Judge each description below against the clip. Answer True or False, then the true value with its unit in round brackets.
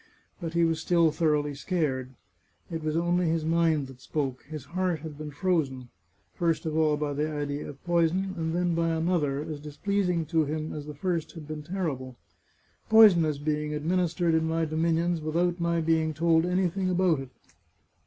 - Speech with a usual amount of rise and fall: False (2.3 semitones)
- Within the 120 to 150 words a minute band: False (185 wpm)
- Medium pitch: True (160 Hz)